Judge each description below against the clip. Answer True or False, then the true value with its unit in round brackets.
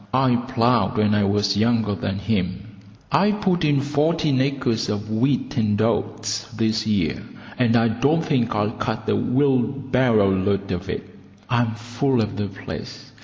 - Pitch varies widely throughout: False (4.1 semitones)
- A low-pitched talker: True (115 Hz)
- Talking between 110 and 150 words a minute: False (160 wpm)